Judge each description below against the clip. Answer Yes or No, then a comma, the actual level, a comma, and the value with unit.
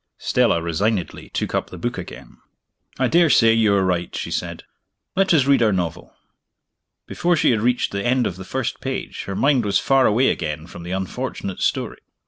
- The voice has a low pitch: Yes, low, 110 Hz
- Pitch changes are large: Yes, wide, 5.9 semitones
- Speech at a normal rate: Yes, average, 190 wpm